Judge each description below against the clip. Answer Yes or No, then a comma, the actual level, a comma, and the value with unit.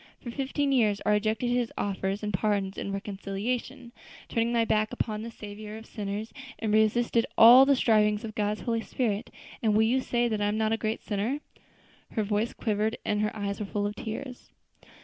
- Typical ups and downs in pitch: No, narrow, 2.2 semitones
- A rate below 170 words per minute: No, average, 195 wpm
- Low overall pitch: No, high, 215 Hz